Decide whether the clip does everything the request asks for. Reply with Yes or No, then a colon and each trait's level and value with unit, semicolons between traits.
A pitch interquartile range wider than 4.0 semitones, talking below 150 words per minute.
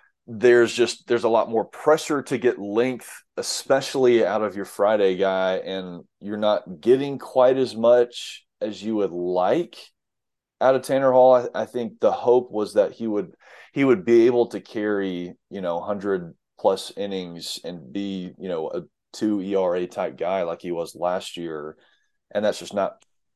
No: average, 4.6 semitones; average, 175 wpm